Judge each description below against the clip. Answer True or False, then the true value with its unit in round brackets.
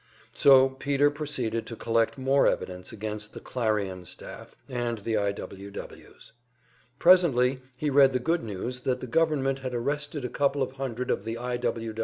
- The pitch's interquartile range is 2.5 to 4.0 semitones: True (3.5 semitones)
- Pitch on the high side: False (125 Hz)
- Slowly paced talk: False (175 wpm)